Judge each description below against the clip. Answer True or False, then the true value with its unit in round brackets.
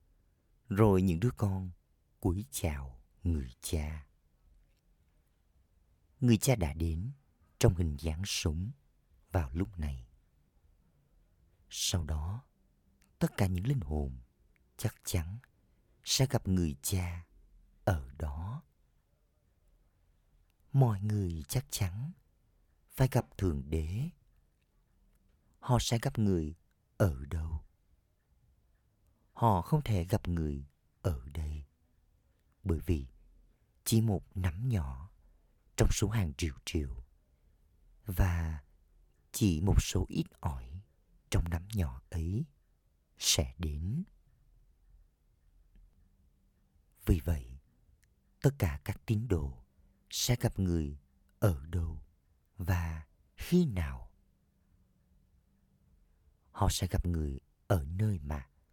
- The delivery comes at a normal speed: False (100 wpm)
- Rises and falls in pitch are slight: False (5.2 semitones)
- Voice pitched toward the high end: False (85 Hz)